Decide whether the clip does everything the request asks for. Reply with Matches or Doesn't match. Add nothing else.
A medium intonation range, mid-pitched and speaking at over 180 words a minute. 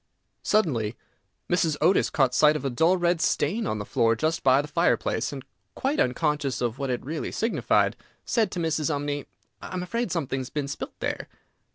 Matches